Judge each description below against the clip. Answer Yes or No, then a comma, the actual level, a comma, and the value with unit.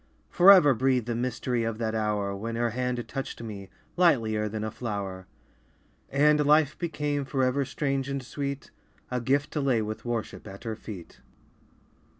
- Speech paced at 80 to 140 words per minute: No, average, 155 wpm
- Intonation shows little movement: No, average, 4.2 semitones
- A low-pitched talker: Yes, low, 125 Hz